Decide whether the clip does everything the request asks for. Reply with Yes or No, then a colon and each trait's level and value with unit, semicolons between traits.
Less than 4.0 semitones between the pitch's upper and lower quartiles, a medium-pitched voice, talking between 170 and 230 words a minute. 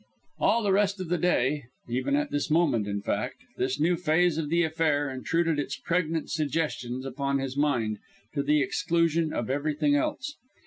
Yes: average, 3.6 semitones; medium, 150 Hz; average, 175 wpm